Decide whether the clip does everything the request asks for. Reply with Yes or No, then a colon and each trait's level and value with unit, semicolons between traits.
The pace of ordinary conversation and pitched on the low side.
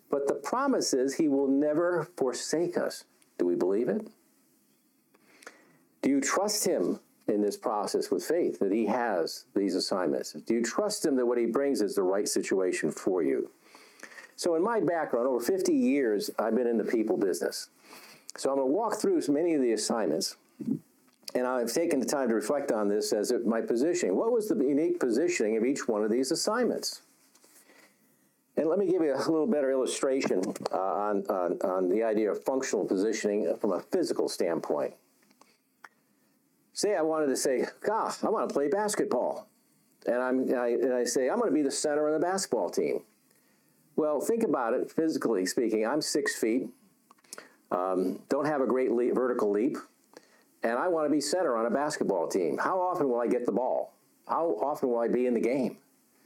No: average, 190 wpm; high, 210 Hz